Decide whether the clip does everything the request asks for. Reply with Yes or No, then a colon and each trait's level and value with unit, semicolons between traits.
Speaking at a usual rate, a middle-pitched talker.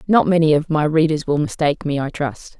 No: fast, 230 wpm; medium, 155 Hz